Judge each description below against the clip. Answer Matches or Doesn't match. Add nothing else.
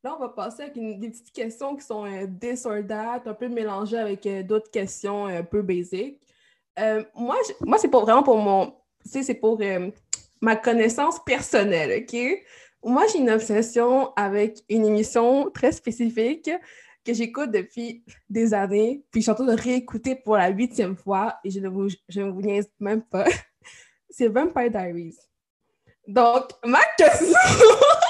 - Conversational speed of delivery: Matches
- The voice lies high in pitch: Matches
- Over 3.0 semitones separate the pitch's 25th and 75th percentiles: Matches